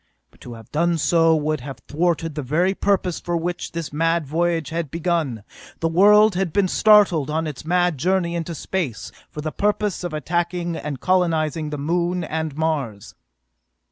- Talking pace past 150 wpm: Yes, average, 175 wpm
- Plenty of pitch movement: No, narrow, 2.6 semitones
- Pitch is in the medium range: Yes, medium, 165 Hz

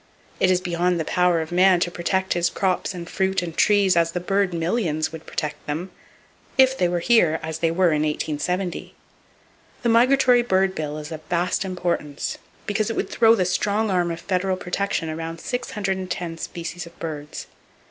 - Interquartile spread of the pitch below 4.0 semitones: Yes, average, 2.7 semitones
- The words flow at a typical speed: Yes, average, 180 wpm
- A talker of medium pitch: Yes, medium, 180 Hz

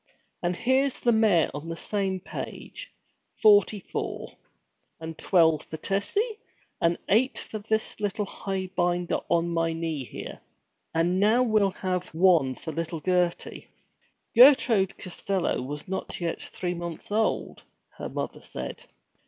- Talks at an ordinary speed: No, slow, 130 wpm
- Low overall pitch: No, medium, 185 Hz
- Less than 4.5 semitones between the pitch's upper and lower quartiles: Yes, average, 4.0 semitones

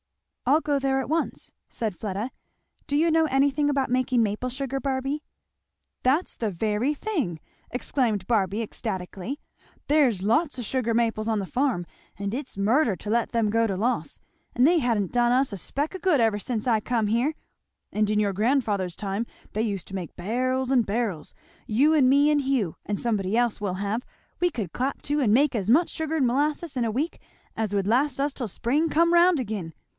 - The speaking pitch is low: No, high, 240 Hz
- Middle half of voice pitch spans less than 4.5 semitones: No, average, 4.9 semitones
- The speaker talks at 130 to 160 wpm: No, average, 200 wpm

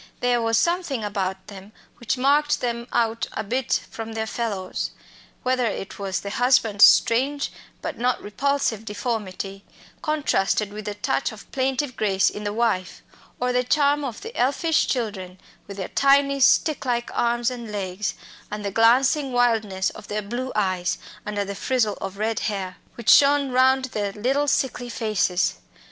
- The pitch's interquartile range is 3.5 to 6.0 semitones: Yes, average, 4.1 semitones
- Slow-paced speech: No, average, 160 wpm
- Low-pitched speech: No, high, 230 Hz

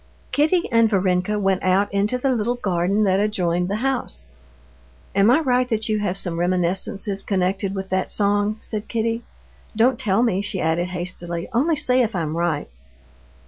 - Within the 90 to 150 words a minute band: No, average, 170 wpm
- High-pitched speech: Yes, high, 200 Hz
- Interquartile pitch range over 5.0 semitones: No, average, 3.8 semitones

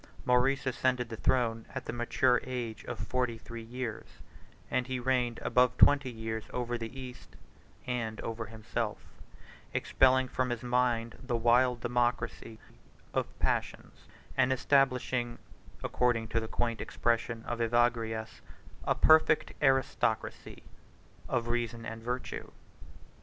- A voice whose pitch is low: Yes, low, 120 Hz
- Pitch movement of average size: No, narrow, 1.7 semitones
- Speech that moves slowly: Yes, slow, 130 wpm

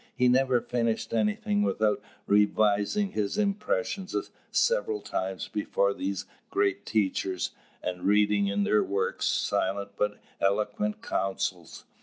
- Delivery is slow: Yes, slow, 115 wpm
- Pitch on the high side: No, low, 105 Hz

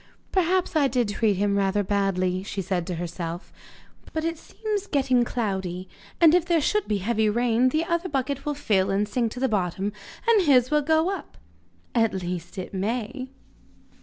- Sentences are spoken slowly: No, average, 180 wpm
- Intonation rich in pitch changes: Yes, wide, 7.4 semitones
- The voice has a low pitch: No, high, 230 Hz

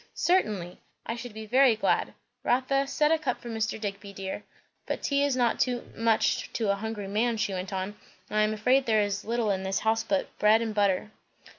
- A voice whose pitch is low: No, high, 220 Hz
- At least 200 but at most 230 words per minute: Yes, fast, 205 wpm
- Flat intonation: No, average, 3.2 semitones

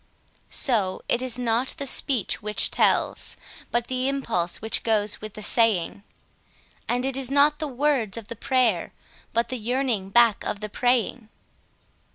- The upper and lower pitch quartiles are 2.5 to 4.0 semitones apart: Yes, average, 3.3 semitones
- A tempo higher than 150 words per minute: Yes, average, 160 wpm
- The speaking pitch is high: Yes, high, 235 Hz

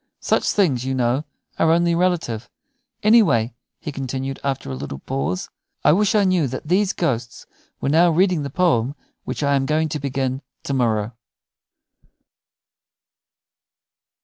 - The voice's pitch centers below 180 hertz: Yes, medium, 140 Hz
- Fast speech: No, average, 145 wpm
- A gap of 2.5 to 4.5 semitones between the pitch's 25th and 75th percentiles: No, average, 5.3 semitones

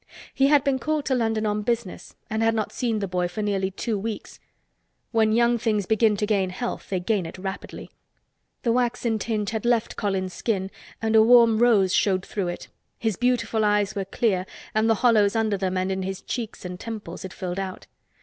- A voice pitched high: Yes, high, 215 Hz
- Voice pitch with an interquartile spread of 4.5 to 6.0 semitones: No, average, 3.1 semitones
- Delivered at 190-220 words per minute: Yes, fast, 205 wpm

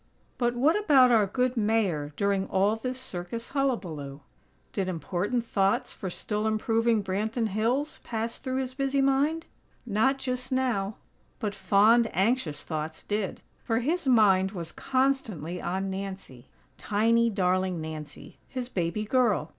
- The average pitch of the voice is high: Yes, high, 215 Hz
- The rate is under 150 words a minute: Yes, average, 140 wpm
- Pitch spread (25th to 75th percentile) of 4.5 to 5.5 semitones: Yes, average, 4.9 semitones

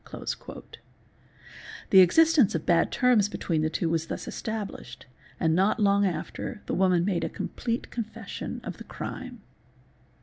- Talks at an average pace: Yes, average, 145 wpm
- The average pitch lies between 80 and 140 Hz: No, high, 195 Hz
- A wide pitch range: No, average, 4.8 semitones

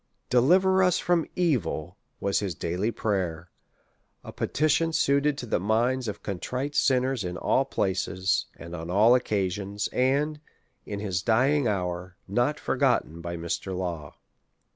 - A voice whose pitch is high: No, low, 105 Hz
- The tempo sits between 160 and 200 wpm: No, average, 140 wpm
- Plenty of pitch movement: Yes, wide, 7.1 semitones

